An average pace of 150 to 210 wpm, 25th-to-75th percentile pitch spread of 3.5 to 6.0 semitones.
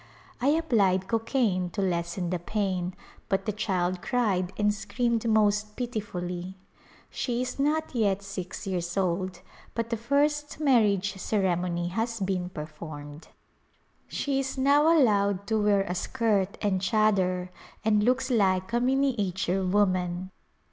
No: slow, 135 wpm; average, 4.2 semitones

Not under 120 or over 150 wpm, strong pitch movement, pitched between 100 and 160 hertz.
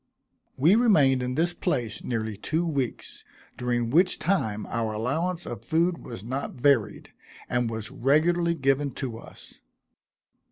Yes: slow, 135 wpm; wide, 6.2 semitones; low, 135 Hz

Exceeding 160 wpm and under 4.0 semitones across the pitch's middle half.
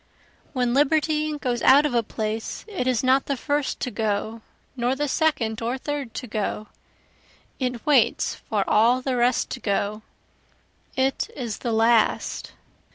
No: average, 155 wpm; average, 3.6 semitones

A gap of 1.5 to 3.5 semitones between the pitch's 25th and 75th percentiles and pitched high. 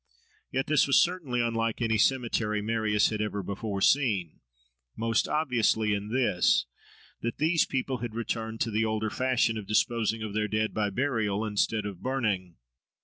No: narrow, 2.6 semitones; low, 110 Hz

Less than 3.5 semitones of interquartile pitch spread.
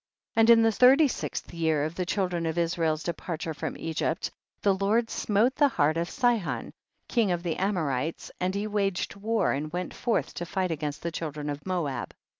No: average, 4.7 semitones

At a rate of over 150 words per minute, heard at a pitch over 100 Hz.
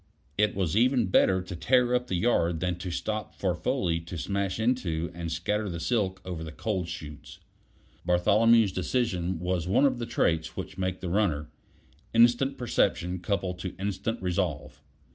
No: average, 165 wpm; very low, 95 Hz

